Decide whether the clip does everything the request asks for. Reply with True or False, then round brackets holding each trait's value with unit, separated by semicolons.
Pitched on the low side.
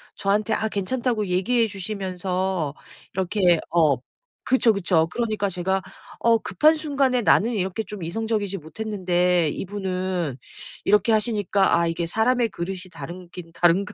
False (195 Hz)